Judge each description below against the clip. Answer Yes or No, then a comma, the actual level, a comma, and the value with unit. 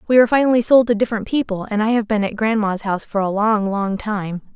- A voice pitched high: Yes, high, 215 Hz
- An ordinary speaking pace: No, fast, 250 wpm